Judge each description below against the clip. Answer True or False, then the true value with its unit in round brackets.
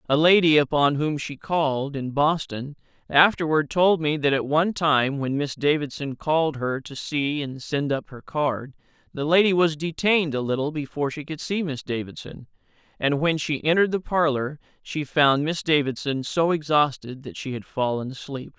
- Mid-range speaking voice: True (145 Hz)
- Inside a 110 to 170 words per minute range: False (180 wpm)